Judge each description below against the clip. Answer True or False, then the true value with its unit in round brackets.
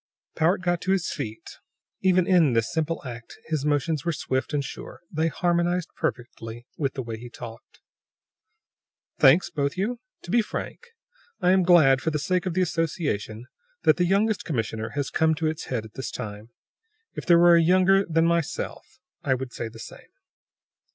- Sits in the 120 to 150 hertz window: False (160 Hz)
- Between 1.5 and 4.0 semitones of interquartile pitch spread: False (5.6 semitones)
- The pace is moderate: True (180 wpm)